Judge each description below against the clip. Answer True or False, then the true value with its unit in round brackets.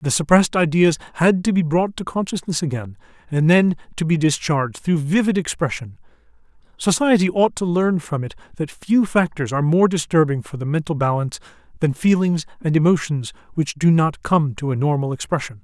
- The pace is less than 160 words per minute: False (175 wpm)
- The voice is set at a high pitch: False (160 Hz)